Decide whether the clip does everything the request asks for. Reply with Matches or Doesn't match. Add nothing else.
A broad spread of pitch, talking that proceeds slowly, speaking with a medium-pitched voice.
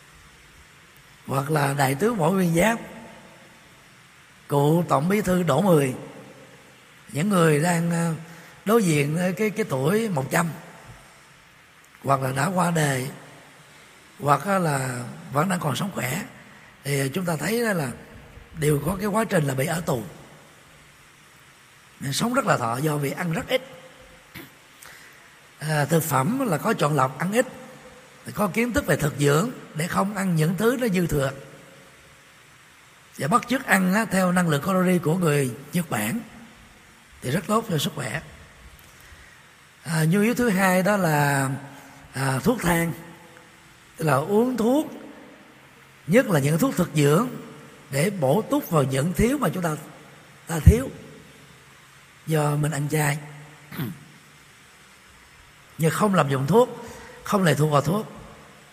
Matches